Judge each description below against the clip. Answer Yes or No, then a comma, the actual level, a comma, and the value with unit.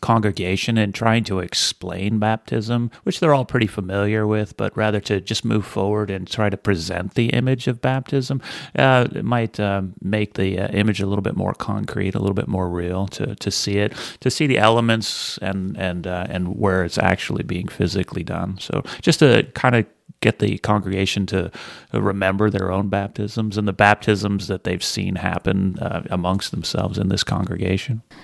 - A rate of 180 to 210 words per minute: Yes, average, 185 wpm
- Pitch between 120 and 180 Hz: No, low, 100 Hz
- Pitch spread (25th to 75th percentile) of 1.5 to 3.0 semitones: Yes, average, 2.7 semitones